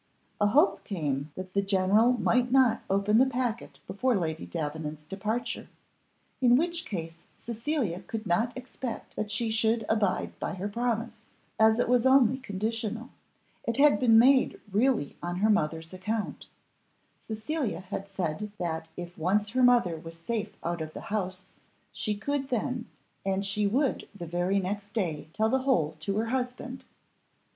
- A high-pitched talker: Yes, high, 215 Hz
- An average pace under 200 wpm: Yes, average, 160 wpm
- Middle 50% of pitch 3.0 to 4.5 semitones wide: No, average, 4.9 semitones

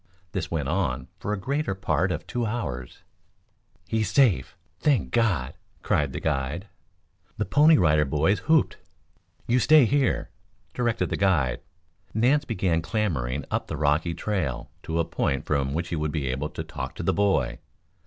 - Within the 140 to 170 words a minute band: Yes, average, 165 wpm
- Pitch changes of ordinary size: No, wide, 7.5 semitones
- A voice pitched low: Yes, very low, 90 Hz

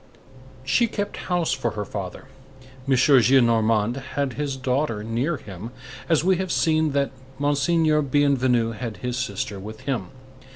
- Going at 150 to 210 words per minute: No, average, 140 wpm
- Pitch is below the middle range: Yes, low, 130 Hz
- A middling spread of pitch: Yes, average, 4.6 semitones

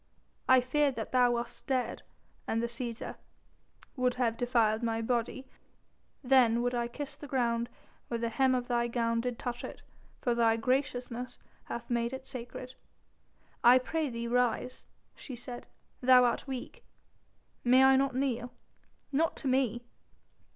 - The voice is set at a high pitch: Yes, high, 245 Hz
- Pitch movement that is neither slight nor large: No, narrow, 1.6 semitones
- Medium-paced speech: Yes, average, 150 wpm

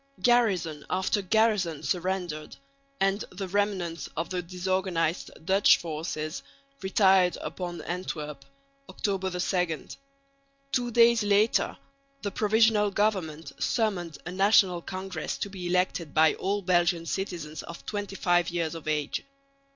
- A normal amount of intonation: Yes, average, 3.1 semitones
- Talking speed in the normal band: No, slow, 120 wpm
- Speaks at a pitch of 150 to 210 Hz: Yes, medium, 185 Hz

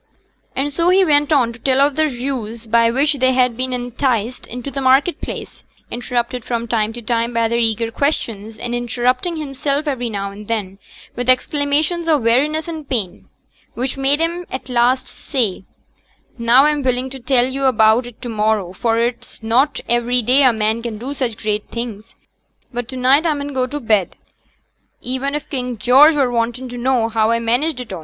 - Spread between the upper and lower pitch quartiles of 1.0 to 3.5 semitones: Yes, average, 3.1 semitones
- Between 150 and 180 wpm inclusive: No, average, 200 wpm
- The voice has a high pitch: Yes, very high, 250 Hz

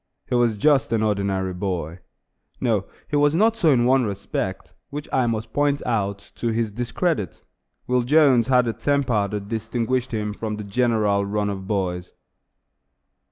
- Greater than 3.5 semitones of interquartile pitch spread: Yes, average, 4.1 semitones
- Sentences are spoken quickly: No, average, 160 wpm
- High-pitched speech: No, low, 115 Hz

